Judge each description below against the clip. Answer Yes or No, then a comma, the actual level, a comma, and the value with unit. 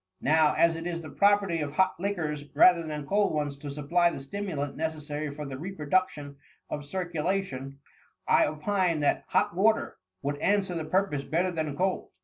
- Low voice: No, medium, 160 Hz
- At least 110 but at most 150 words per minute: No, average, 175 wpm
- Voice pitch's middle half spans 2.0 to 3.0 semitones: No, average, 4.1 semitones